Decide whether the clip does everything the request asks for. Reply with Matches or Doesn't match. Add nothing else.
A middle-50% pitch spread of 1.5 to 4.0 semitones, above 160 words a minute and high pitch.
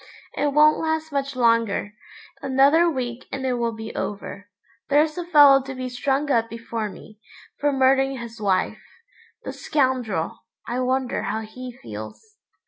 Doesn't match